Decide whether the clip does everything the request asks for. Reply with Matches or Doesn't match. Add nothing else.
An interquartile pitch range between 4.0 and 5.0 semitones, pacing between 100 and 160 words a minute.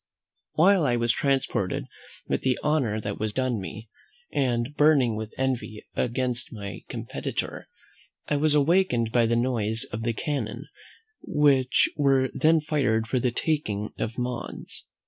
Matches